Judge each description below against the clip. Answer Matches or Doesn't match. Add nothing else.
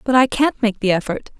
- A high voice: Matches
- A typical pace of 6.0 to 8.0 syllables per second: Doesn't match